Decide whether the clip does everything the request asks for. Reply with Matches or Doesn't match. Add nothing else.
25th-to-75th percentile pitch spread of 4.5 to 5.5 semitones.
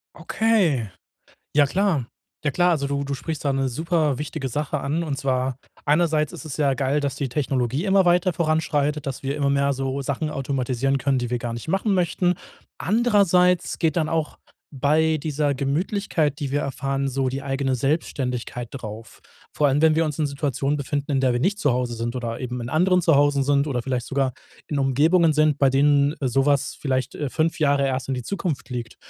Doesn't match